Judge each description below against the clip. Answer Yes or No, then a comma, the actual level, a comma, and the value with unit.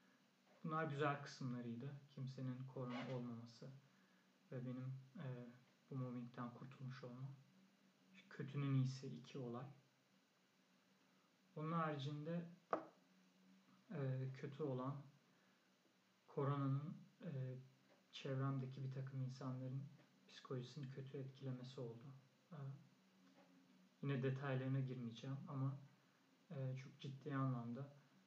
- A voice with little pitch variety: Yes, narrow, 2.1 semitones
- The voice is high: No, low, 135 Hz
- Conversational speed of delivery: No, slow, 85 wpm